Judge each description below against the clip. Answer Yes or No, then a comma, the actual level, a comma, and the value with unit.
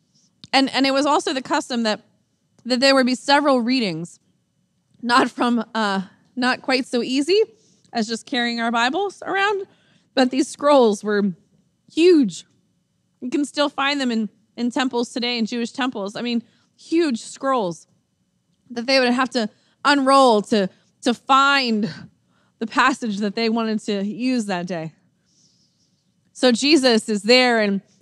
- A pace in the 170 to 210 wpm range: No, average, 150 wpm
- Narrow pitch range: No, average, 3.9 semitones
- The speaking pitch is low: No, high, 240 Hz